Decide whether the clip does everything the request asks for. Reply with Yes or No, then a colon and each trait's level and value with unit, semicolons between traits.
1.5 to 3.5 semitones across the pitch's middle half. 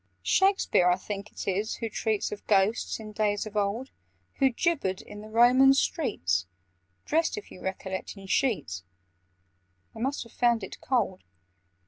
No: average, 4.4 semitones